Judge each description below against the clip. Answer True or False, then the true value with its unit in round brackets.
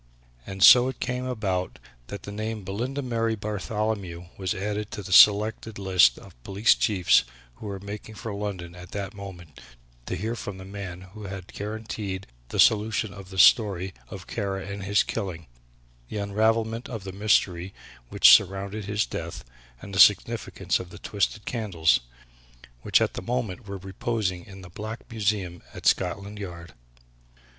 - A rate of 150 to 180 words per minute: True (165 wpm)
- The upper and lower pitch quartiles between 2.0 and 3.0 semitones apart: True (2.4 semitones)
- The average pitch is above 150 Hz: False (100 Hz)